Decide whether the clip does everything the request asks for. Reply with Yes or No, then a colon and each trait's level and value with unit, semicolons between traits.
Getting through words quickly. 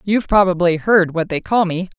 Yes: fast, 210 wpm